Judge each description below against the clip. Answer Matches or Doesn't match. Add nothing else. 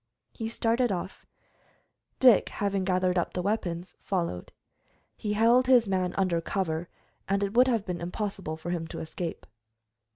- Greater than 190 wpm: Doesn't match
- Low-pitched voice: Doesn't match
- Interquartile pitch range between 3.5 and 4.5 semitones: Matches